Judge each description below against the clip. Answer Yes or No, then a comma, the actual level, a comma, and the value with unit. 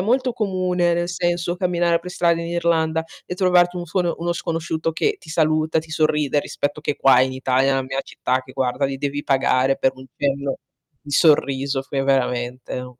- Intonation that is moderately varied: Yes, average, 4.3 semitones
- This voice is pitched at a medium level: Yes, medium, 155 Hz